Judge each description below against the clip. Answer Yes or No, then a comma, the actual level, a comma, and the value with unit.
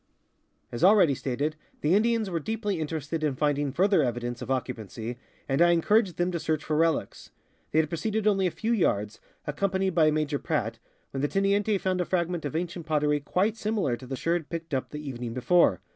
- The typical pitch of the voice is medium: Yes, medium, 160 Hz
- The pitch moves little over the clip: No, average, 4.9 semitones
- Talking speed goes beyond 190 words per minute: Yes, fast, 205 wpm